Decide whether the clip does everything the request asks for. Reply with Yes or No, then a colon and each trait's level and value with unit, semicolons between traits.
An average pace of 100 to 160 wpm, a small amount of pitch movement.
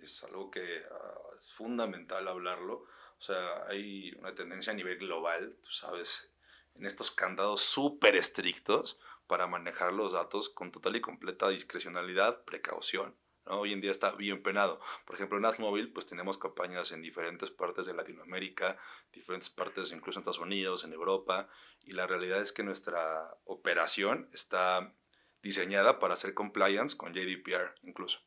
Yes: average, 155 wpm; narrow, 2.1 semitones